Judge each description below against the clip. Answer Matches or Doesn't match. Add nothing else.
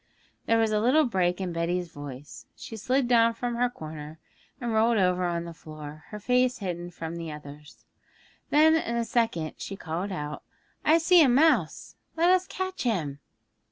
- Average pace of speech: Matches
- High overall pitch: Matches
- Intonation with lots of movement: Matches